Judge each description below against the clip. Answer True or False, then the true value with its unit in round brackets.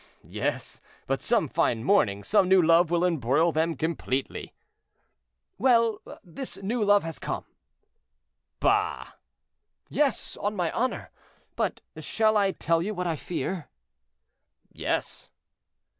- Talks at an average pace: False (120 wpm)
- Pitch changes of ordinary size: True (4.4 semitones)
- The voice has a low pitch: False (180 Hz)